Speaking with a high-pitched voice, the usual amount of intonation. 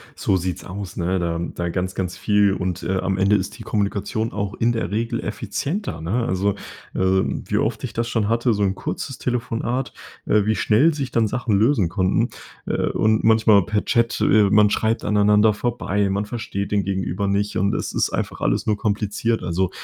No: low, 105 Hz; average, 3.0 semitones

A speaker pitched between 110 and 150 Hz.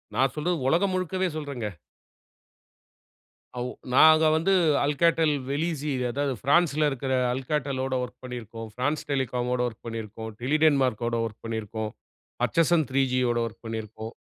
Yes: low, 135 Hz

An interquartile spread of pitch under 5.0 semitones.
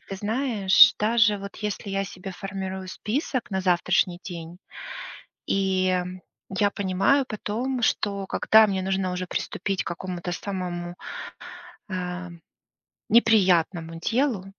Yes: narrow, 2.5 semitones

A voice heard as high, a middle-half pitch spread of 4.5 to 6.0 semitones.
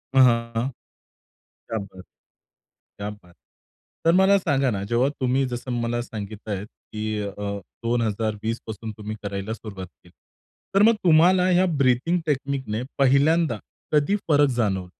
No: low, 115 Hz; average, 5.1 semitones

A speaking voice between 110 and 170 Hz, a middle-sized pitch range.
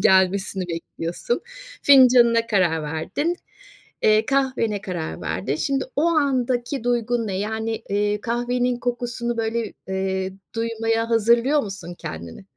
No: high, 225 Hz; average, 4.2 semitones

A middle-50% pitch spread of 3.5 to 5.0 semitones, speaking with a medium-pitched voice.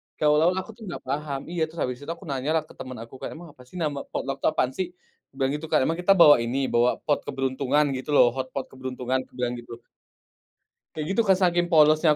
Yes: average, 3.9 semitones; medium, 145 Hz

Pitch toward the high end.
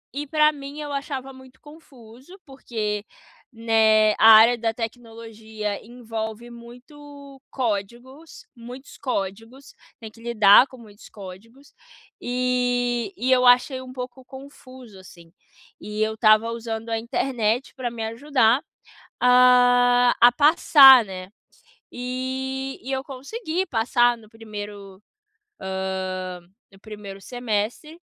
Yes: high, 240 Hz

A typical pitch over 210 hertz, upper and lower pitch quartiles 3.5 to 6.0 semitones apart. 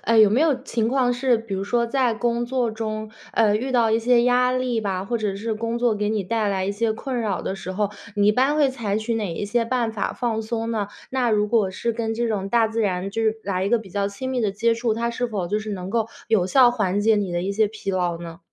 No: high, 220 Hz; average, 2.7 semitones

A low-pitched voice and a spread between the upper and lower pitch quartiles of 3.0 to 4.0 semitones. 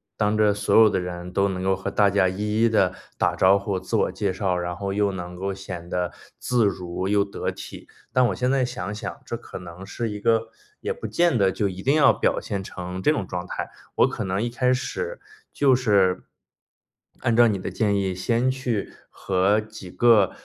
Yes: low, 100 Hz; average, 3.7 semitones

